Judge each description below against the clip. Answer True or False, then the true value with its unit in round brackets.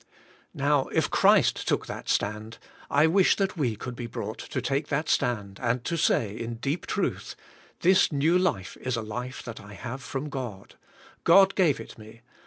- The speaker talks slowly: False (185 wpm)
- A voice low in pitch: True (125 Hz)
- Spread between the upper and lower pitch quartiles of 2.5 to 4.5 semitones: False (5.3 semitones)